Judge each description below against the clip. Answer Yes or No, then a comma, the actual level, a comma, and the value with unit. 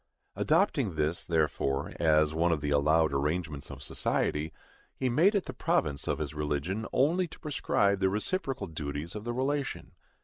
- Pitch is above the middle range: No, very low, 80 Hz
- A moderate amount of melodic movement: No, wide, 8.1 semitones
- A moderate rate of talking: Yes, average, 165 wpm